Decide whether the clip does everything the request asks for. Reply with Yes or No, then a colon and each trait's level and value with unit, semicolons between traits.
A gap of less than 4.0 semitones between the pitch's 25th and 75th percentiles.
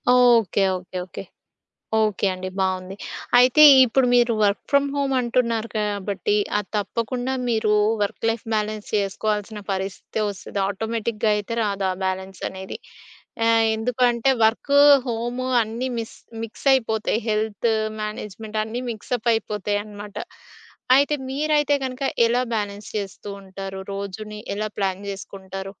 Yes: average, 2.9 semitones